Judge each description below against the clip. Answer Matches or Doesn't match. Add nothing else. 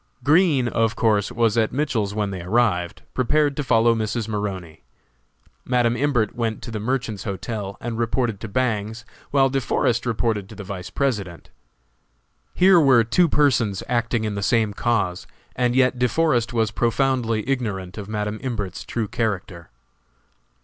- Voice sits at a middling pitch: Doesn't match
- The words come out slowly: Doesn't match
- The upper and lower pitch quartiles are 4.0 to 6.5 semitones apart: Doesn't match